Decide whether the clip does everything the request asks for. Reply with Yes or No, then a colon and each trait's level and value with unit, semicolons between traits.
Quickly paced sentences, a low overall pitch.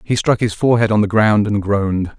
Yes: fast, 245 wpm; low, 105 Hz